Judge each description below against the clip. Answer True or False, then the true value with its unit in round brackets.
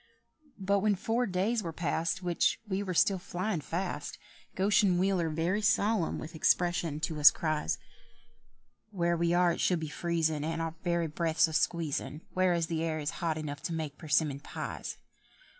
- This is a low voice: False (170 Hz)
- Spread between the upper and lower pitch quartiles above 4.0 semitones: False (2.7 semitones)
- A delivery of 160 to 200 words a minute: True (170 wpm)